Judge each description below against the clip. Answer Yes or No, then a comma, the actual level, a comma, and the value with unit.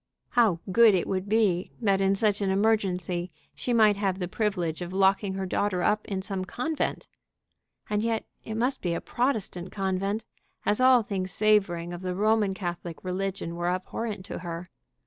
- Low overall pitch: No, high, 195 Hz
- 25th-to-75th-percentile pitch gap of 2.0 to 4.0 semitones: Yes, average, 2.8 semitones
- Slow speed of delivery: No, average, 175 wpm